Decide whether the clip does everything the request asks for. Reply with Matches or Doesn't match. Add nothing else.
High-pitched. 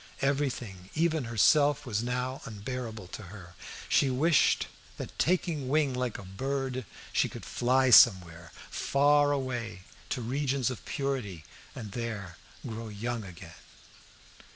Doesn't match